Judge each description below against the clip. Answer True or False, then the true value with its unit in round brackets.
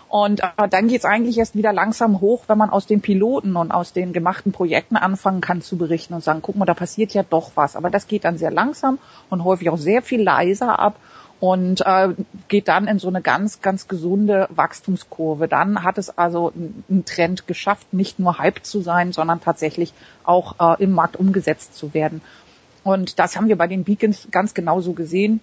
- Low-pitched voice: False (190 Hz)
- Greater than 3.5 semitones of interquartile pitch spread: False (3.2 semitones)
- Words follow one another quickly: True (210 wpm)